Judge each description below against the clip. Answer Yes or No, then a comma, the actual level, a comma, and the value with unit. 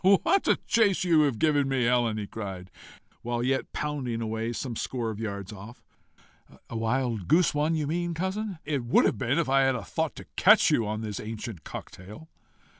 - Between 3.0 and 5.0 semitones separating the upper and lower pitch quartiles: No, wide, 5.5 semitones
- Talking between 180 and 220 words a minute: Yes, average, 190 wpm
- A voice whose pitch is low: Yes, low, 125 Hz